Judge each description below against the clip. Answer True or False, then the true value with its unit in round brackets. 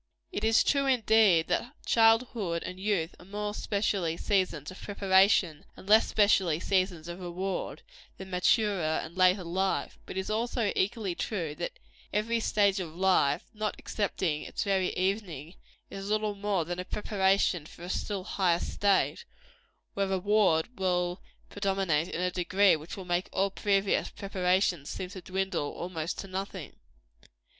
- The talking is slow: False (155 wpm)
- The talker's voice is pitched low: False (190 Hz)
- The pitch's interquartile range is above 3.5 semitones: False (2.7 semitones)